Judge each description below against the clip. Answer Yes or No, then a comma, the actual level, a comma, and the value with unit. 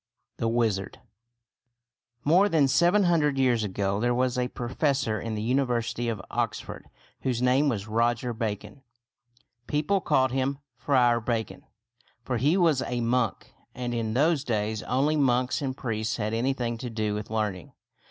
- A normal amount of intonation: Yes, average, 3.4 semitones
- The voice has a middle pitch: No, low, 120 Hz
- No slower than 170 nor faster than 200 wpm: No, average, 150 wpm